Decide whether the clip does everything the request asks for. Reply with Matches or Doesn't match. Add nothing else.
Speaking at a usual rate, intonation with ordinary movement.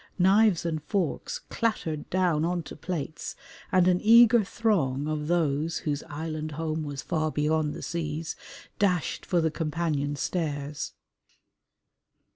Doesn't match